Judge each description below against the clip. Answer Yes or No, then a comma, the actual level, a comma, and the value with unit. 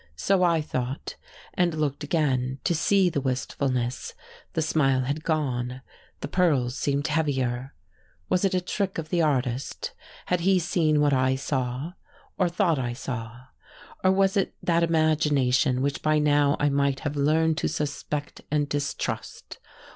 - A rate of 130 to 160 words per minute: Yes, average, 155 wpm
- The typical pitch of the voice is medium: Yes, medium, 145 Hz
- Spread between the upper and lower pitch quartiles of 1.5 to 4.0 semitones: Yes, average, 3.7 semitones